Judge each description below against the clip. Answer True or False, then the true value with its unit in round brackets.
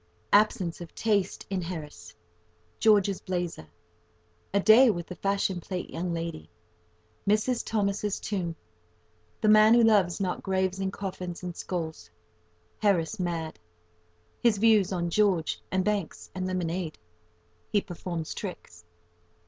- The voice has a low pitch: False (175 Hz)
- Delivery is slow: True (105 wpm)